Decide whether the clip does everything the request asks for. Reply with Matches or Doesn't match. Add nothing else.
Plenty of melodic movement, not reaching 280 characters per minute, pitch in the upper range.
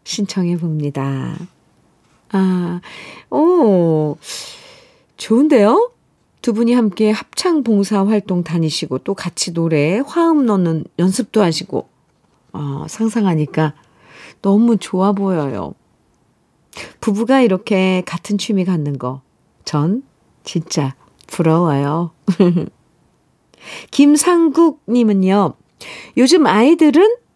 Matches